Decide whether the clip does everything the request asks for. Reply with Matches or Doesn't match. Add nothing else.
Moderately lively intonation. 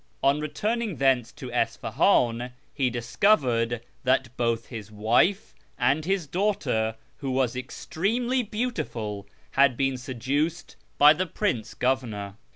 Doesn't match